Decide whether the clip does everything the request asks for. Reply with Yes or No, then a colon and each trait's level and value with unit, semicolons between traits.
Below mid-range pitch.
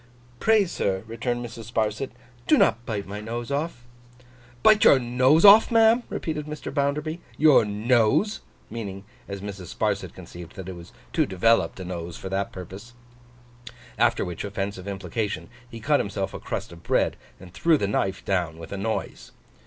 Yes: low, 110 Hz